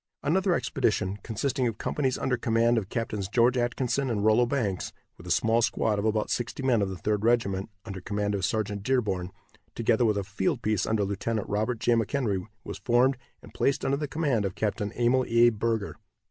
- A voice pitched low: Yes, low, 115 Hz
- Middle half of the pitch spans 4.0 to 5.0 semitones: No, average, 3.3 semitones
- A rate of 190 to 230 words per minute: Yes, average, 195 wpm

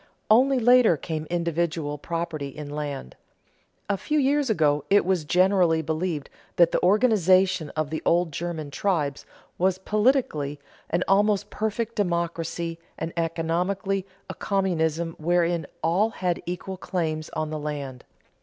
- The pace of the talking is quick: No, slow, 135 wpm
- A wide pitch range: No, average, 3.8 semitones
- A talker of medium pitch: Yes, medium, 170 Hz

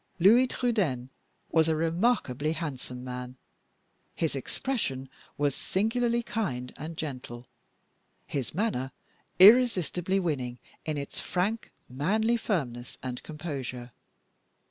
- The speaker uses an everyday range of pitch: No, wide, 8.2 semitones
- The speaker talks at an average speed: No, slow, 100 wpm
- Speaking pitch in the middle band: Yes, medium, 155 Hz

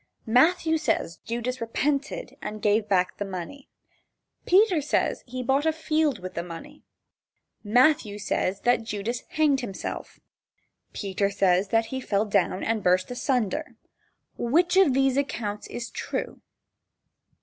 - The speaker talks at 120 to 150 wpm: Yes, average, 140 wpm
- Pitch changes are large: Yes, wide, 5.9 semitones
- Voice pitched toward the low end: No, high, 240 Hz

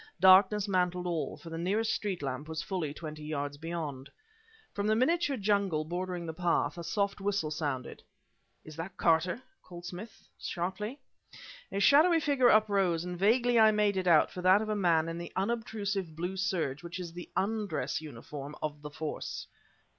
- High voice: No, medium, 180 Hz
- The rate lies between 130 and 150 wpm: No, average, 175 wpm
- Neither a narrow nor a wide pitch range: Yes, average, 4.3 semitones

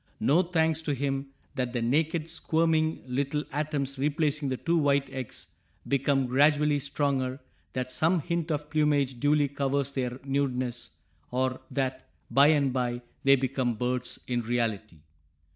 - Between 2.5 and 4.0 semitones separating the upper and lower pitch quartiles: Yes, average, 2.8 semitones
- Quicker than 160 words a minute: No, average, 145 wpm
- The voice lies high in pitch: No, medium, 140 Hz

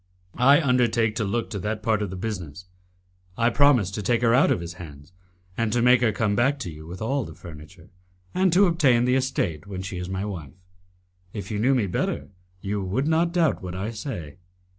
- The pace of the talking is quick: Yes, fast, 215 wpm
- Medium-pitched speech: No, low, 105 Hz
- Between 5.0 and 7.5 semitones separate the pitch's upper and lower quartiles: Yes, wide, 5.5 semitones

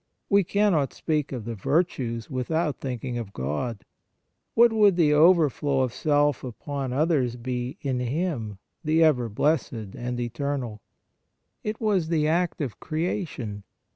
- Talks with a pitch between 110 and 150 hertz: Yes, medium, 140 Hz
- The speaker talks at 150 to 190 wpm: No, average, 140 wpm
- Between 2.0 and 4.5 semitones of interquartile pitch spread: No, average, 5.1 semitones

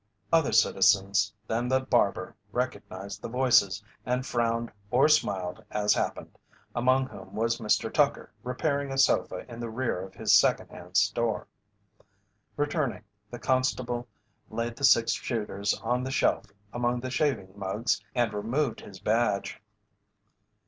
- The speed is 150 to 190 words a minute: No, average, 140 wpm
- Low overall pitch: Yes, low, 120 Hz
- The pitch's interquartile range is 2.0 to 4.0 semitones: Yes, average, 3.7 semitones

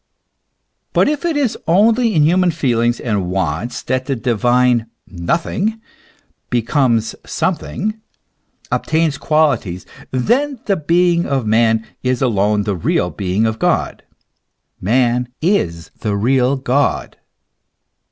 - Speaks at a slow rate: Yes, slow, 120 wpm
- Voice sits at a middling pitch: No, low, 125 Hz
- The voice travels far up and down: Yes, wide, 7.3 semitones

